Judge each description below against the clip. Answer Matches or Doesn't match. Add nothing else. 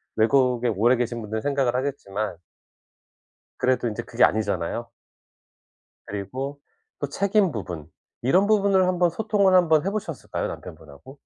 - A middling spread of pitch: Doesn't match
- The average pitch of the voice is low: Matches